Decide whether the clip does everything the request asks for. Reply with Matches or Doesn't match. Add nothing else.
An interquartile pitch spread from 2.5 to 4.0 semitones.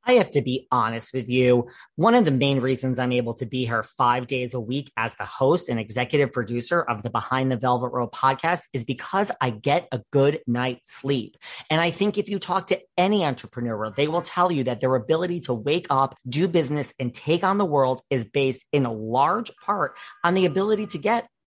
Doesn't match